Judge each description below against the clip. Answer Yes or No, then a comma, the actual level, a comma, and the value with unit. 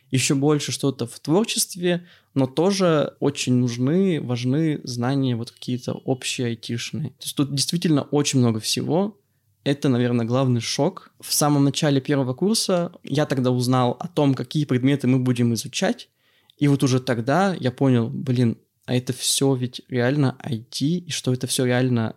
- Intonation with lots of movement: No, average, 3.0 semitones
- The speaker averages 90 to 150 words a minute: No, fast, 160 wpm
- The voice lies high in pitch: No, low, 135 Hz